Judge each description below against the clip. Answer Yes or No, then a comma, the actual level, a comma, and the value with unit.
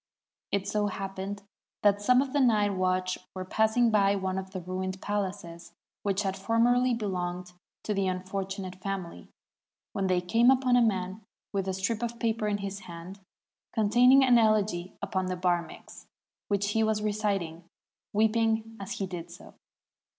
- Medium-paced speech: Yes, average, 165 wpm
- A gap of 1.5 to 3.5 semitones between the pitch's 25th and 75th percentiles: Yes, average, 2.8 semitones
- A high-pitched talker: Yes, high, 200 Hz